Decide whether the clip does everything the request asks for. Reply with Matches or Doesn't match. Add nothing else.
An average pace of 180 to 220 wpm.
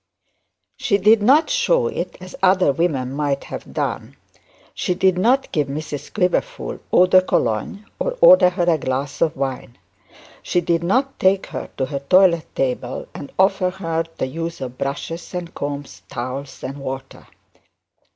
Doesn't match